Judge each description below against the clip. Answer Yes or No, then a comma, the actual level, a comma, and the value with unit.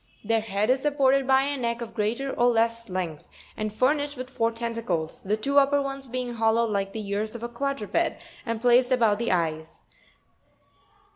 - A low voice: No, high, 230 Hz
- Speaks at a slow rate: No, fast, 205 wpm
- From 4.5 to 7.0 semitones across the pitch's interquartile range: No, average, 3.6 semitones